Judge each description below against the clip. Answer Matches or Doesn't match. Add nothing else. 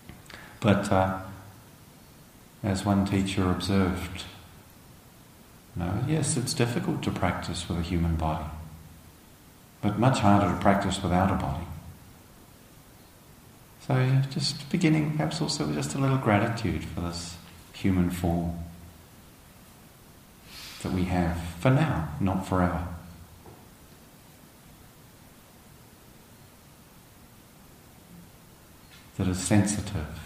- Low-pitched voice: Matches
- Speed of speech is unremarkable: Doesn't match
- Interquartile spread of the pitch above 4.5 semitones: Matches